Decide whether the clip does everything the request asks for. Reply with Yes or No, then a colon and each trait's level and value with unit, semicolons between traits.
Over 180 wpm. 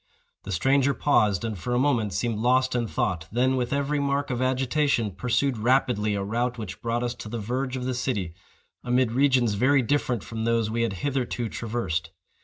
Yes: average, 195 wpm